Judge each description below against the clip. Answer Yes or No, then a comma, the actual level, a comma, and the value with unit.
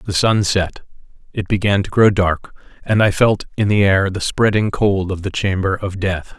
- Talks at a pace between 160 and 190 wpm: No, fast, 205 wpm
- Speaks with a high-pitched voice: No, low, 100 Hz